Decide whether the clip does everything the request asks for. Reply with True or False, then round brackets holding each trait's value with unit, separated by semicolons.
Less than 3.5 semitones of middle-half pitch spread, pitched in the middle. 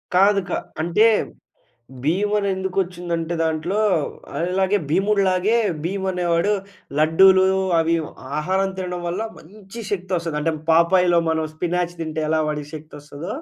True (2.8 semitones; 180 Hz)